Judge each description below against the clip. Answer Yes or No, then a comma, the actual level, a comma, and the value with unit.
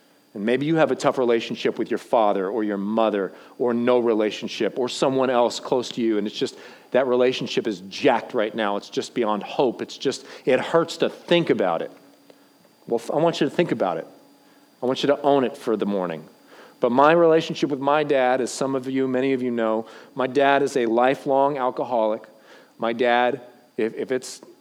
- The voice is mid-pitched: No, low, 125 Hz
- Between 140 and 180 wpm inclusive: No, fast, 205 wpm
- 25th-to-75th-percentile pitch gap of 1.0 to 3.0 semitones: No, average, 3.5 semitones